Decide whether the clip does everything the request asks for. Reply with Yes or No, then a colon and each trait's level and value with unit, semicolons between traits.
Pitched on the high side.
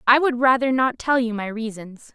Yes: high, 240 Hz